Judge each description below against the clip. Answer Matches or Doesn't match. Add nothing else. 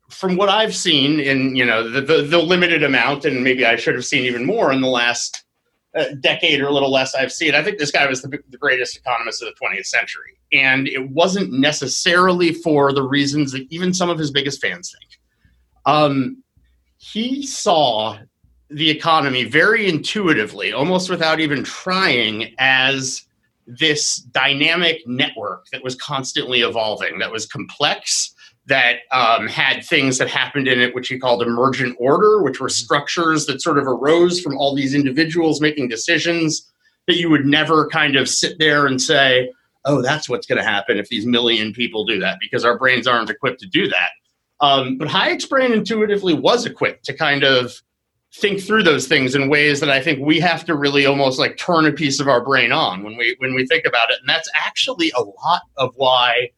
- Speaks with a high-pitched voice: Doesn't match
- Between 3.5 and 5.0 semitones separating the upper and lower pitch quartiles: Matches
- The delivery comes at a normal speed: Matches